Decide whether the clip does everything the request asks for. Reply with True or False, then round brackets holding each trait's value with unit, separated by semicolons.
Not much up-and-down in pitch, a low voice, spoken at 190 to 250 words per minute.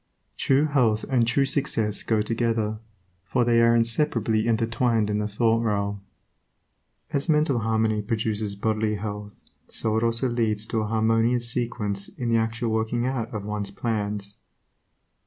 False (1.8 semitones; 110 Hz; 150 wpm)